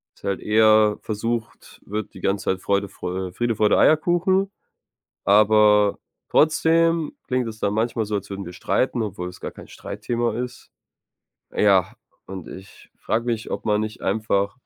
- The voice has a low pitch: Yes, low, 110 Hz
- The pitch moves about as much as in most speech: Yes, average, 3.1 semitones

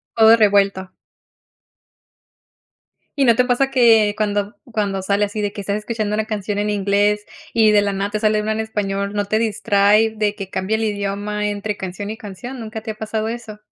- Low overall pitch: No, high, 210 Hz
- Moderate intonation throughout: No, narrow, 1.5 semitones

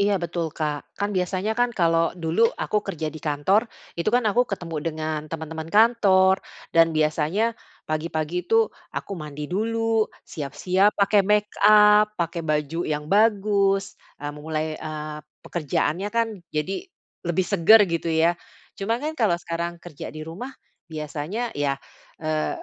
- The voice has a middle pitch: Yes, medium, 170 Hz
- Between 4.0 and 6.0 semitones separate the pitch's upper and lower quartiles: Yes, average, 4.7 semitones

